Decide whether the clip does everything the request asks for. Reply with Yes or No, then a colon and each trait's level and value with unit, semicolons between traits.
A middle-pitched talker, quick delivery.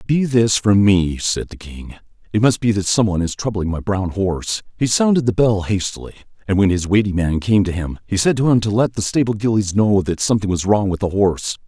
No: low, 100 Hz; fast, 245 wpm